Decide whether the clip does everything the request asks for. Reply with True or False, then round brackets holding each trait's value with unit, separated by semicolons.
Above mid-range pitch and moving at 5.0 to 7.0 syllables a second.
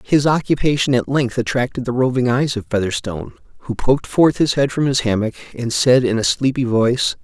False (125 Hz; 5.6 syllables/s)